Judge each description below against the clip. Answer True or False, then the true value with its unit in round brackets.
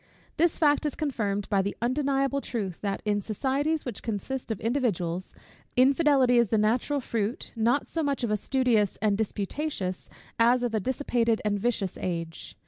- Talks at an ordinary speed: True (165 wpm)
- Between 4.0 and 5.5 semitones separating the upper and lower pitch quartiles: True (4.8 semitones)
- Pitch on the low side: False (235 Hz)